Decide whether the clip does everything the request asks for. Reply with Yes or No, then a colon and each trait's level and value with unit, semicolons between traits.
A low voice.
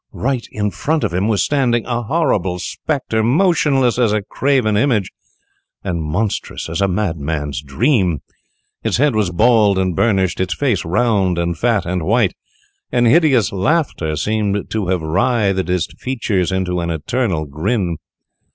Yes: low, 105 Hz